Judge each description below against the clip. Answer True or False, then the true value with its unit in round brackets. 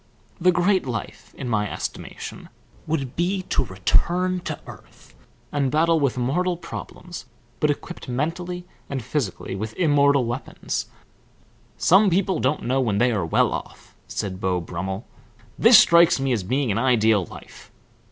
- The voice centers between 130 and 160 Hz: True (135 Hz)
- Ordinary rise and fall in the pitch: False (7.5 semitones)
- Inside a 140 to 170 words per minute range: True (150 wpm)